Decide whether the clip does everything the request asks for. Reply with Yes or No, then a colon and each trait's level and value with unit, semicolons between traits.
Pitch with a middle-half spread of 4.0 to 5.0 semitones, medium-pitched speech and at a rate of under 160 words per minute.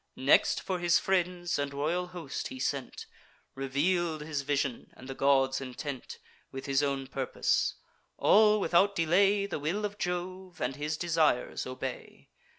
Yes: average, 4.7 semitones; medium, 155 Hz; average, 150 wpm